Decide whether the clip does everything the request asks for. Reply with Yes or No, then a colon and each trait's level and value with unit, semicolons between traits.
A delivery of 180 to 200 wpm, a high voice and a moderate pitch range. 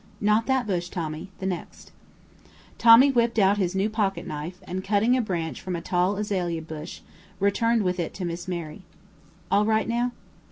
No: average, 170 wpm; high, 195 Hz; average, 3.8 semitones